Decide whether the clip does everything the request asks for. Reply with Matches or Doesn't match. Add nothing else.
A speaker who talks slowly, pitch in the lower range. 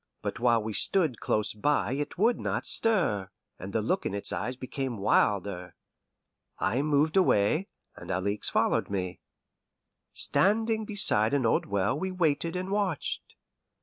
Doesn't match